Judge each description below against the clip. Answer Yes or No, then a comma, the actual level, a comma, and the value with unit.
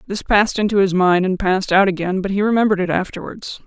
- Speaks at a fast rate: Yes, fast, 230 wpm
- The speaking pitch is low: No, high, 190 Hz